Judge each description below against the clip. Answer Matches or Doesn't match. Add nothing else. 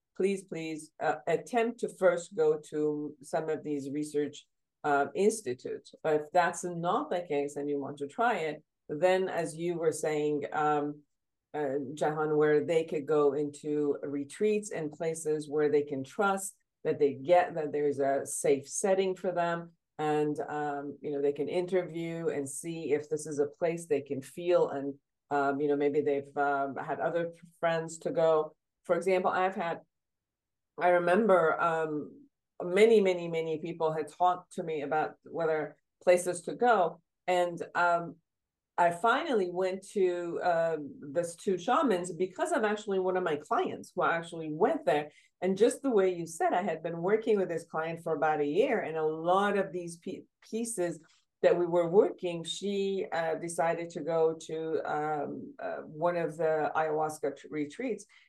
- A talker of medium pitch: Matches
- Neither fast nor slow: Matches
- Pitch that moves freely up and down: Doesn't match